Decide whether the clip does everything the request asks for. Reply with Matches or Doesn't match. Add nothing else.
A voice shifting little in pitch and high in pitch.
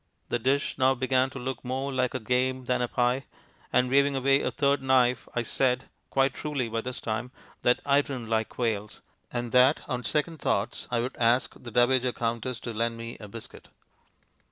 Doesn't match